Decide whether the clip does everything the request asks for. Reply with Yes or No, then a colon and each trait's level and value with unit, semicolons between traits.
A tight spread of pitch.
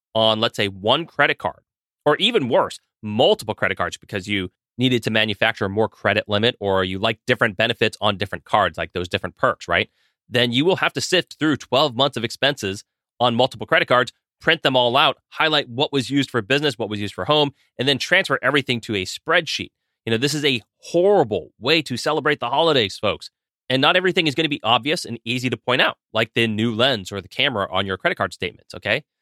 No: average, 4.6 semitones